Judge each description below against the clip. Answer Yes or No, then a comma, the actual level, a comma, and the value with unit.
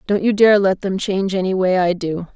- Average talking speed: No, fast, 255 wpm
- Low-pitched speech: No, high, 190 Hz